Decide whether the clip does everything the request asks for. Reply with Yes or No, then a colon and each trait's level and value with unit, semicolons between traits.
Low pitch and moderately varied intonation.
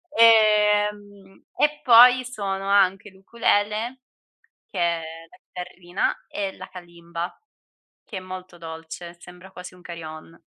No: high, 190 Hz; average, 3.1 semitones